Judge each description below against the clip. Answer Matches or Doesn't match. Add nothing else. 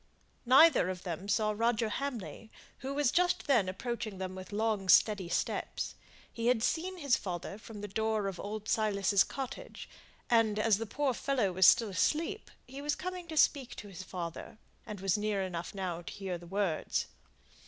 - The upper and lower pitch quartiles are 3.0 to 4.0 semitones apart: Doesn't match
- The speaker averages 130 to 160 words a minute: Doesn't match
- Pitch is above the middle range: Matches